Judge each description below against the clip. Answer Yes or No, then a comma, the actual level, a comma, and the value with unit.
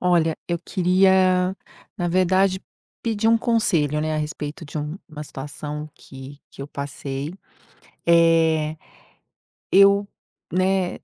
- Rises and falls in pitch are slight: No, average, 3.8 semitones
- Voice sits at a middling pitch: Yes, medium, 170 Hz